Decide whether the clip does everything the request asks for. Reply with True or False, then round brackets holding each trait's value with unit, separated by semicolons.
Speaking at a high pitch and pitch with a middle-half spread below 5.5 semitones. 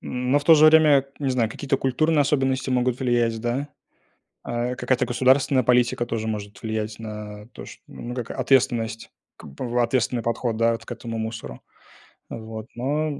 False (120 Hz; 2.7 semitones)